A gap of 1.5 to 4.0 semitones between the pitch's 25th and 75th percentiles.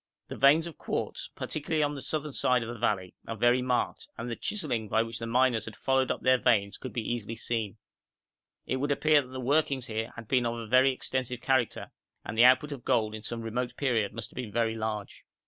Yes: average, 2.7 semitones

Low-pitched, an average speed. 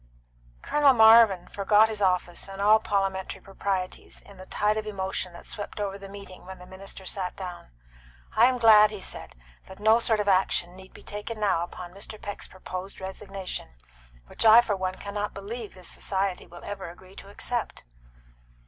No: high, 195 Hz; average, 180 wpm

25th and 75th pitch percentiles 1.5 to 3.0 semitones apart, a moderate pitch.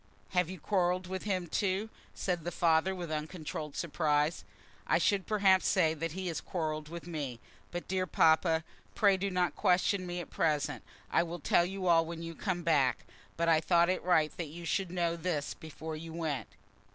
Yes: narrow, 2.5 semitones; medium, 170 Hz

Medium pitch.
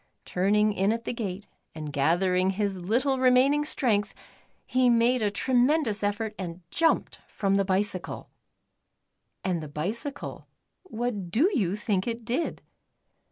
No: high, 210 Hz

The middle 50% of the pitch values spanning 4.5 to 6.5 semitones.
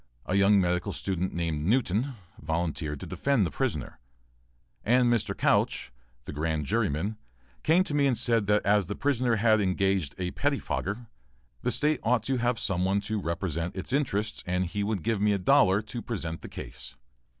Yes: average, 5.1 semitones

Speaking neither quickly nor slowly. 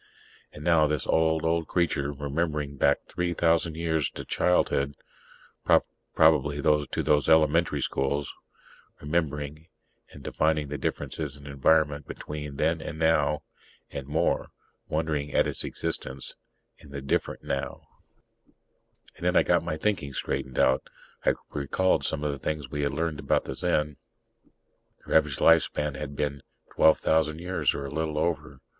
Yes: average, 150 wpm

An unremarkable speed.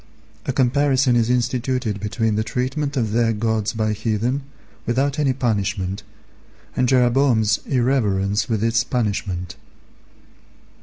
No: slow, 115 wpm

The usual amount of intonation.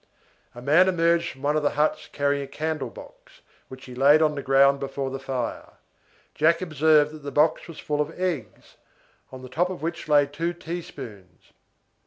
Yes: average, 3.4 semitones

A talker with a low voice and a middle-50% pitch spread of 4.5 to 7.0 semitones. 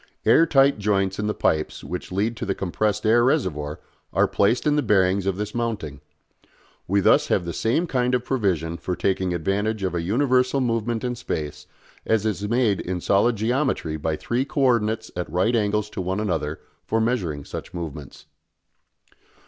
Yes: low, 105 Hz; average, 4.8 semitones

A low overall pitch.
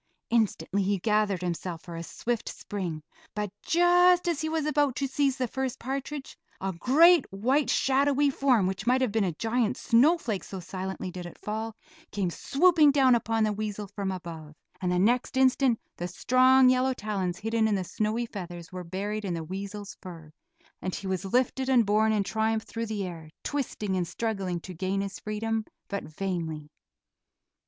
No: high, 215 Hz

